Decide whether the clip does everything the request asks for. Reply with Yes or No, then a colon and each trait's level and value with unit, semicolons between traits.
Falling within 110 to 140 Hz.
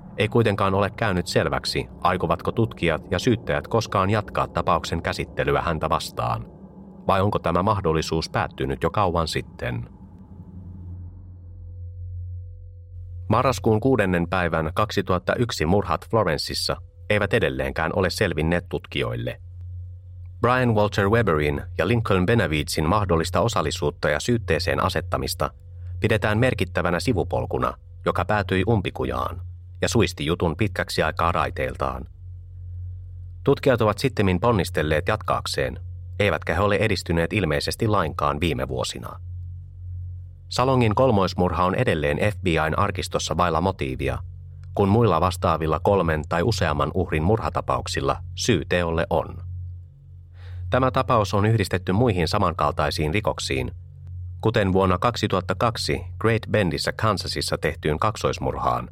No: very low, 90 Hz